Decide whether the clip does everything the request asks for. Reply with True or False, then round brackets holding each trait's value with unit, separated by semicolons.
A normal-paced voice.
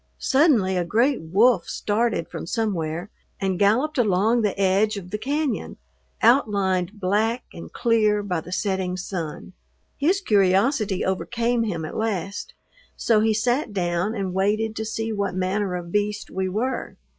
True (150 wpm)